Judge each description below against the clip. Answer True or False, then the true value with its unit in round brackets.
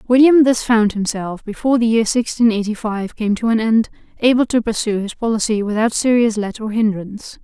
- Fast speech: False (195 wpm)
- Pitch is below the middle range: False (220 Hz)